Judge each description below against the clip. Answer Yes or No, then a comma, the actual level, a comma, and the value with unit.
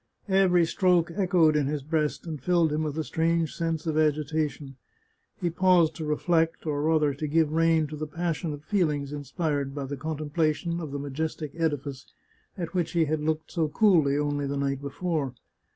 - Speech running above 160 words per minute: Yes, average, 180 wpm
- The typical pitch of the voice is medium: Yes, medium, 155 Hz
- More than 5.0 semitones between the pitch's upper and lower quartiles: No, narrow, 2.4 semitones